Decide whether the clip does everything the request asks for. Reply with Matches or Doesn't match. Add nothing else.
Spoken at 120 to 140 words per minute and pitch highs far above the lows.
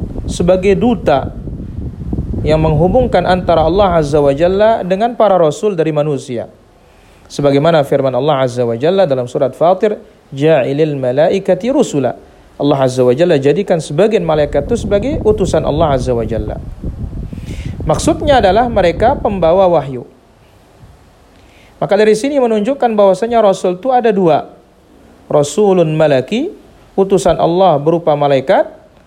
Matches